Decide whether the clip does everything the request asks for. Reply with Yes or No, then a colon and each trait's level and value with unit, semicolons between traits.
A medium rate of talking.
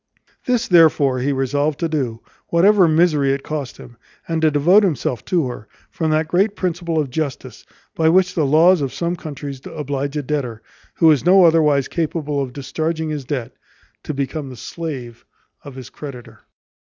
Yes: average, 175 wpm